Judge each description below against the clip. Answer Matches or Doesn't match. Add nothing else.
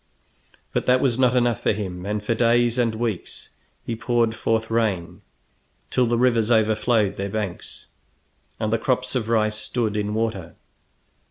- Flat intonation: Matches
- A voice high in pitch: Doesn't match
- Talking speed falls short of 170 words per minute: Matches